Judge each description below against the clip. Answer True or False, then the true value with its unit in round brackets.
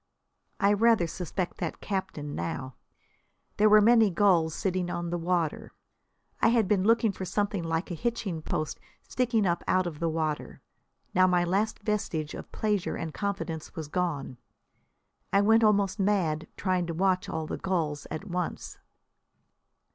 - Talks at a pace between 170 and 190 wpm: False (155 wpm)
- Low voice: False (185 Hz)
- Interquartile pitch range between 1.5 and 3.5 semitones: False (3.9 semitones)